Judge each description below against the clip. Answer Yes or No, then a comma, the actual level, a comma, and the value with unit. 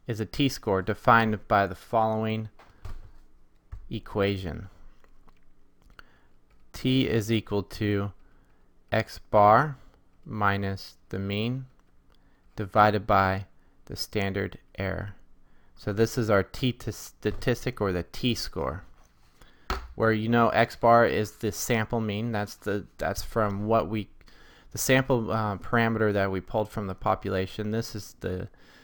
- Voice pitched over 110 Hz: No, low, 105 Hz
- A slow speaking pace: Yes, slow, 120 wpm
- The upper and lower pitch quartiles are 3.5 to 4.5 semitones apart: No, average, 2.8 semitones